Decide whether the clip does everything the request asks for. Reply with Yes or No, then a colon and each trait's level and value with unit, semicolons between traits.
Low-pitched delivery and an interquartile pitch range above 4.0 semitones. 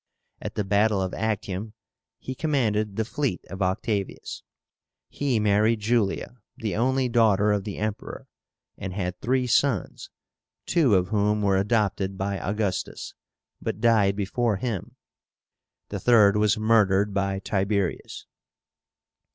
No: low, 105 Hz; narrow, 2.6 semitones